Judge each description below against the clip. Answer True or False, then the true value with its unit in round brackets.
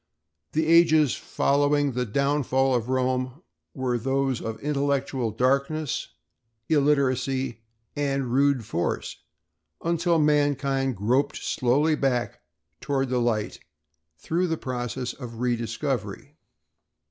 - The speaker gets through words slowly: True (100 wpm)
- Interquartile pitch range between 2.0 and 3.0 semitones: True (2.7 semitones)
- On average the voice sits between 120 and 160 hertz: True (135 Hz)